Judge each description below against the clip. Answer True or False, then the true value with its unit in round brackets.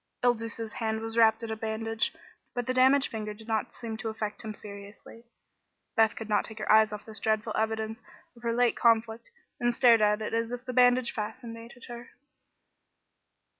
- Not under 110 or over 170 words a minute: False (190 wpm)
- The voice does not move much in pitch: True (1.4 semitones)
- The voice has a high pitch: True (225 Hz)